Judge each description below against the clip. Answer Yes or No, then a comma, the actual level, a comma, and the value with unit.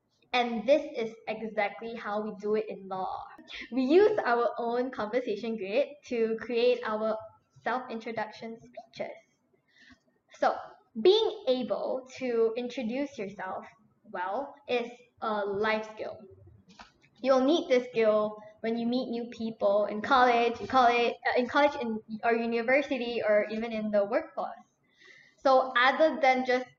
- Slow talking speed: Yes, slow, 130 wpm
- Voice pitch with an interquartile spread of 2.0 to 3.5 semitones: Yes, average, 3.0 semitones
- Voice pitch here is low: No, high, 235 Hz